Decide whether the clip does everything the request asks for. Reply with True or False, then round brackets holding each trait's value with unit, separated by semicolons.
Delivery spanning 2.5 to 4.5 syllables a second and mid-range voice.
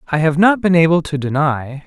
False (5.6 syllables/s; 160 Hz)